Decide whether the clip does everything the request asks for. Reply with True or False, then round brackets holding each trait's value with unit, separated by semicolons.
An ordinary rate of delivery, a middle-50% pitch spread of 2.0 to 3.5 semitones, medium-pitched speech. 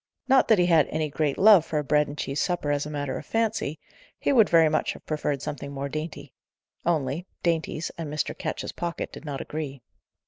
False (210 wpm; 2.9 semitones; 155 Hz)